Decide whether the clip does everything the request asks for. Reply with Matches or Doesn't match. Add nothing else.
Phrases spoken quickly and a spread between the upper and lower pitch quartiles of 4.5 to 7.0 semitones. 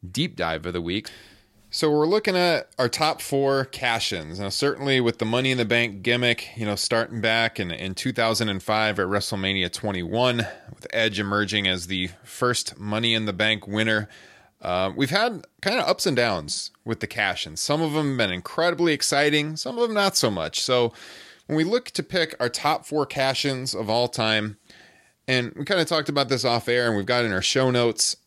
Matches